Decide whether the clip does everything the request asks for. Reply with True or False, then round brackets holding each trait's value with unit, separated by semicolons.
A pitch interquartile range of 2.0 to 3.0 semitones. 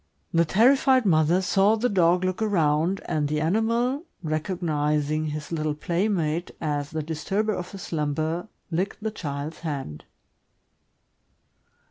False (4.5 semitones)